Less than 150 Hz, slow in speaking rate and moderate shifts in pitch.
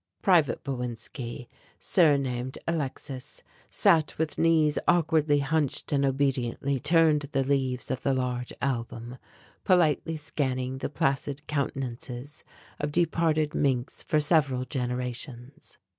Yes: medium, 140 Hz; slow, 110 wpm; average, 3.2 semitones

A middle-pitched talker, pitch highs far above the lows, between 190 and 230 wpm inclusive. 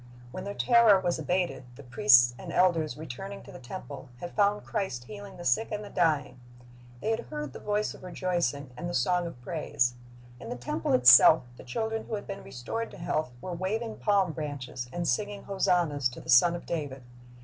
Yes: medium, 170 Hz; wide, 7.0 semitones; average, 200 wpm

